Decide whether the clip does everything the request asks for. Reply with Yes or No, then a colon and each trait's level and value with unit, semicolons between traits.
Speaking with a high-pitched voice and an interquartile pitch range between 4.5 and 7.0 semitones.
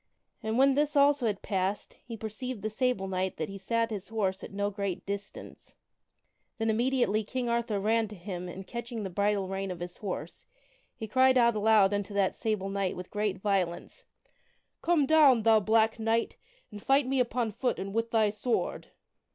No: high, 215 Hz; average, 3.2 semitones